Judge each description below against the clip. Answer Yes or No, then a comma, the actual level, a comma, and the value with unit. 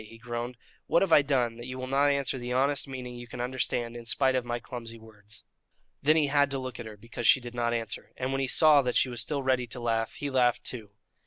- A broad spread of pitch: No, narrow, 2.4 semitones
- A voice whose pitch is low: Yes, low, 125 Hz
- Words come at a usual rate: No, fast, 260 wpm